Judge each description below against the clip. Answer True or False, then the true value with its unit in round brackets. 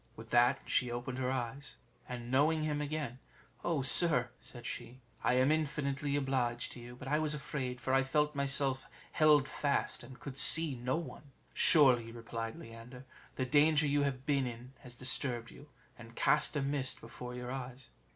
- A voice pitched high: False (130 Hz)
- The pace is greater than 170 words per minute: True (180 wpm)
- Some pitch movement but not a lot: True (3.0 semitones)